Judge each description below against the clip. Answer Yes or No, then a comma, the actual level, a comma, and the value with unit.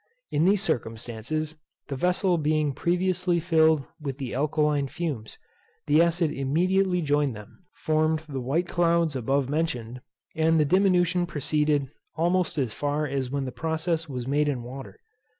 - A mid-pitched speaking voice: Yes, medium, 155 Hz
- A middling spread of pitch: Yes, average, 3.9 semitones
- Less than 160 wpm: Yes, average, 150 wpm